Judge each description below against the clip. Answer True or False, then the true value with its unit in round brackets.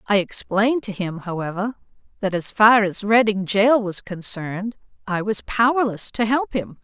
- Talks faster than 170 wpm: False (165 wpm)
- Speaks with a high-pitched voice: True (210 Hz)